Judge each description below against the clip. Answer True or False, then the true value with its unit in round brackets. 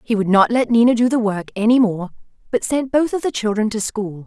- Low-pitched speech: False (225 Hz)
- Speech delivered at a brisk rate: True (255 wpm)